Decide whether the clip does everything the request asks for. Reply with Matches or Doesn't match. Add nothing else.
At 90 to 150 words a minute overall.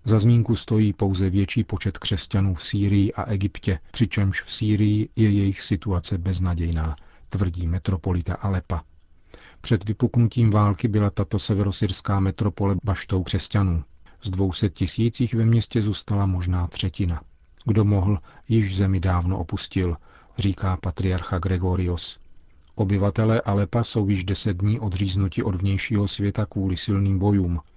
Matches